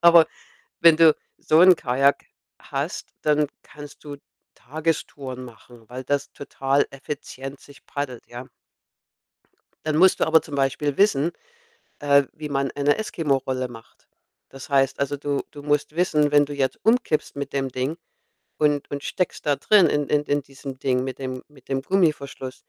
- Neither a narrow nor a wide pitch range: No, narrow, 2.0 semitones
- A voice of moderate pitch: Yes, medium, 145 Hz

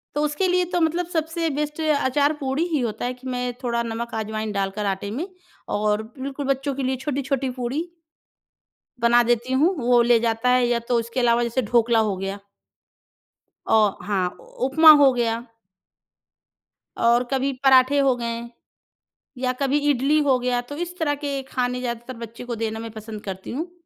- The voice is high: Yes, very high, 250 Hz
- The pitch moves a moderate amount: Yes, average, 3.2 semitones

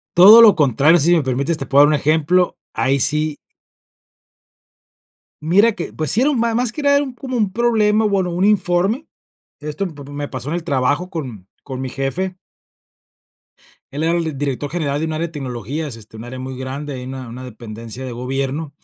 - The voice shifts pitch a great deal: Yes, wide, 5.8 semitones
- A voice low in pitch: No, medium, 150 Hz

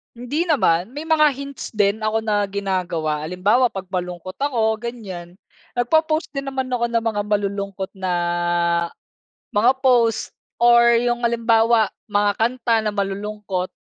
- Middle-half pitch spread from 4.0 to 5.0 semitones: No, average, 3.5 semitones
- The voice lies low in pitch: No, high, 220 Hz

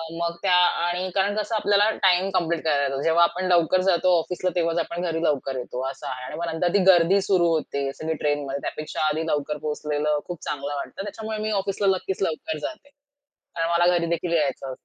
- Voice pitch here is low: No, medium, 170 Hz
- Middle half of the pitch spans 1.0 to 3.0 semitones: No, average, 3.6 semitones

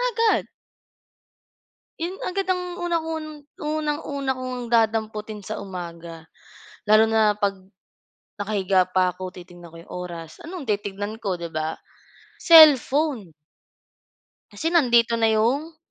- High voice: Yes, high, 220 Hz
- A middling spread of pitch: No, wide, 8.1 semitones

